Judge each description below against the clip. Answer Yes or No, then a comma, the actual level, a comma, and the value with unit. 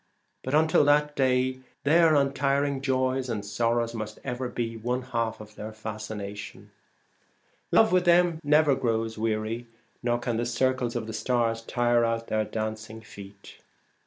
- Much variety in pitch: No, average, 3.2 semitones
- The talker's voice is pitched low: Yes, low, 120 Hz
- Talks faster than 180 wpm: No, average, 155 wpm